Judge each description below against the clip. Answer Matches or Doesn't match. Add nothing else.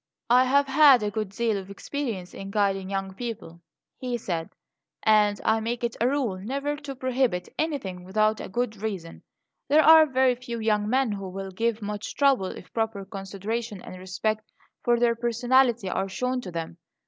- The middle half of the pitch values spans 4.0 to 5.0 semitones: Matches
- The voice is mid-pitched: Doesn't match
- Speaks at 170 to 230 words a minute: Matches